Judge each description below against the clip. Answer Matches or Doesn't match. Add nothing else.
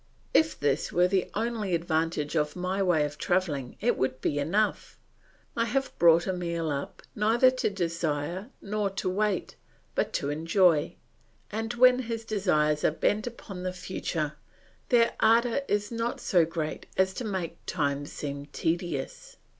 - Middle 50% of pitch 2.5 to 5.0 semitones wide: Doesn't match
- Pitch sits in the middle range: Matches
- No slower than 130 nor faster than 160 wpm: Matches